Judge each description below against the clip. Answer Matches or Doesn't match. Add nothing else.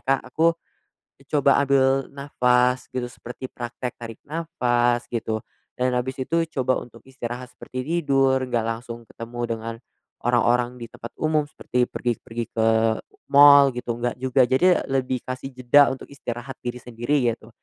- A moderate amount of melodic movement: Doesn't match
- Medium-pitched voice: Doesn't match